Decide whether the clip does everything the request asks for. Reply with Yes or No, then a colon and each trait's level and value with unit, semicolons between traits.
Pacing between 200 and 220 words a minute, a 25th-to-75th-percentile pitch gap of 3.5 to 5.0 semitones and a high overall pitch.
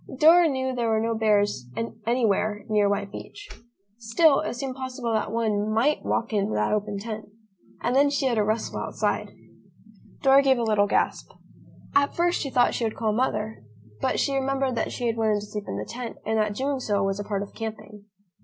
Yes: fast, 205 wpm; average, 3.9 semitones; high, 225 Hz